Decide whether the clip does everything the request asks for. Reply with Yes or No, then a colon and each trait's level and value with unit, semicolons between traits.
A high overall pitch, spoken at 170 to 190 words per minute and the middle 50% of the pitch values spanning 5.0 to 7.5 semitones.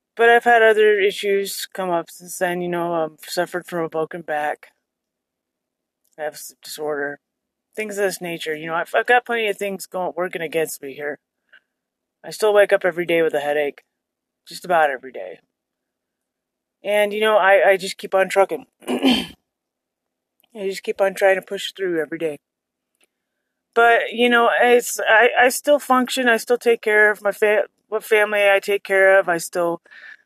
No: high, 195 Hz; average, 185 wpm; average, 4.2 semitones